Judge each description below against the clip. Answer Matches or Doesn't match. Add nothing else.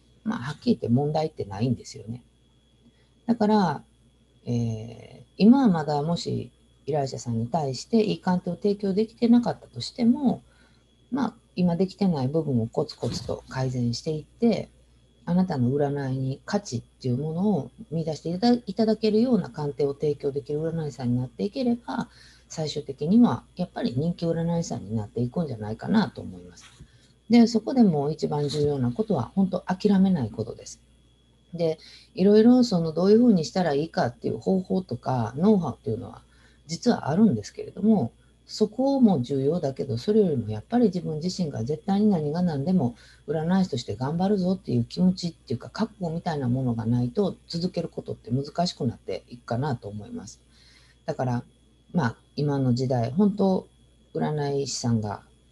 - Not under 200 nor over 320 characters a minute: Doesn't match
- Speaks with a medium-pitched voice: Matches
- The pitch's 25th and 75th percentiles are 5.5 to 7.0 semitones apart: Doesn't match